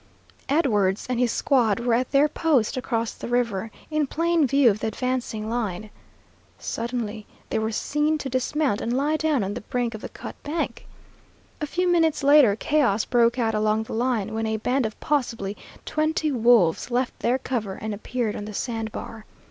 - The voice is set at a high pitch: Yes, high, 240 Hz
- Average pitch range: Yes, average, 4.4 semitones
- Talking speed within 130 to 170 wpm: No, average, 185 wpm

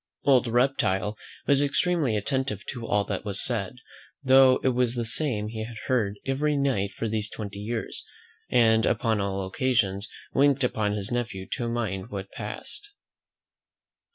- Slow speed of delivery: No, average, 155 wpm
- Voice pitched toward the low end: Yes, low, 115 Hz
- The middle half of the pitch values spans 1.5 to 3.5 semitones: No, average, 4.0 semitones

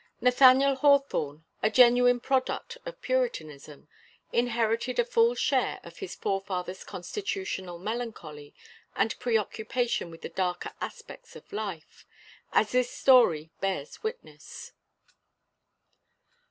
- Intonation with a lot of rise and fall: Yes, wide, 6.3 semitones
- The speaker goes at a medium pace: No, slow, 105 wpm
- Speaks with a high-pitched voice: Yes, high, 230 Hz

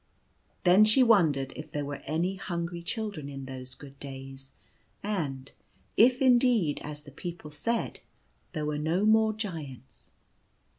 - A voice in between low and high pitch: Yes, medium, 160 Hz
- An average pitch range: No, wide, 7.0 semitones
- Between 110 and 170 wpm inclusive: Yes, average, 140 wpm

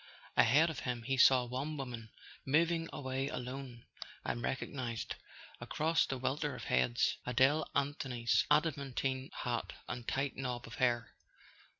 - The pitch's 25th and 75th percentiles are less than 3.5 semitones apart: Yes, average, 2.7 semitones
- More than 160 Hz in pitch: No, low, 130 Hz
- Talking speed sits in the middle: No, slow, 130 wpm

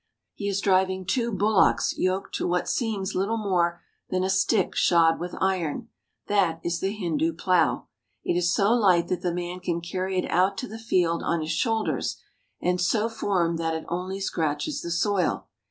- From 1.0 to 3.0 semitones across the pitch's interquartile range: Yes, narrow, 2.6 semitones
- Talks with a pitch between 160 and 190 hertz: Yes, medium, 185 Hz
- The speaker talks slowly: No, average, 185 wpm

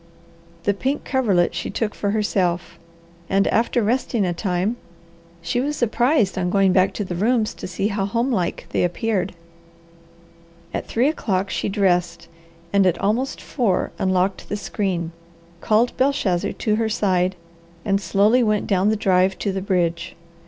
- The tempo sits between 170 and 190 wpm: No, average, 155 wpm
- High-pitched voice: Yes, high, 200 Hz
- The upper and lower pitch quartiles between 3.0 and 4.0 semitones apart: Yes, average, 3.4 semitones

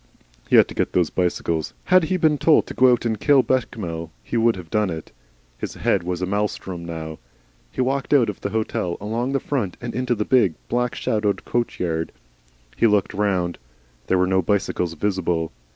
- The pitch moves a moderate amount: No, wide, 5.7 semitones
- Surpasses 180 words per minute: Yes, average, 200 wpm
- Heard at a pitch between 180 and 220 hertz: No, low, 105 Hz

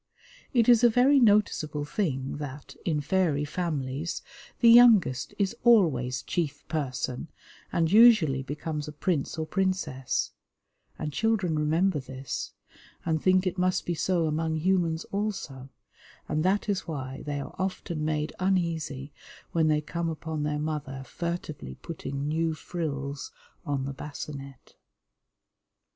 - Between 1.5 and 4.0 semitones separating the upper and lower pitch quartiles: No, average, 4.4 semitones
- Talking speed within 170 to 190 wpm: No, slow, 135 wpm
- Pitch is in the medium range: Yes, medium, 155 Hz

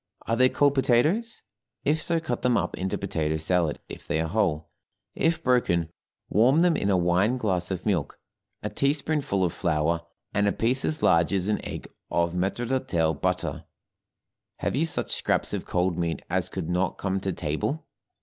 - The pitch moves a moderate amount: No, wide, 7.2 semitones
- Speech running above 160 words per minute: Yes, average, 180 wpm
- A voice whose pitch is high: No, very low, 95 Hz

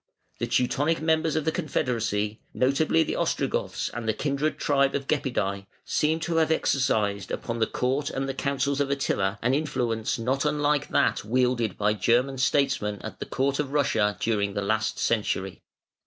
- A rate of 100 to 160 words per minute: No, average, 170 wpm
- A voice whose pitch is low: Yes, low, 130 Hz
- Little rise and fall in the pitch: No, average, 4.7 semitones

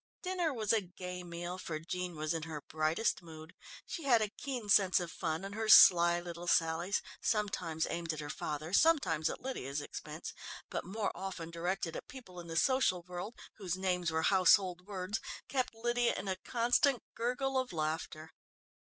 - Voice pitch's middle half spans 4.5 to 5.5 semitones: Yes, average, 5.1 semitones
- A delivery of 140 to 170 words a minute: No, average, 180 wpm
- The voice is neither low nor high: Yes, medium, 180 Hz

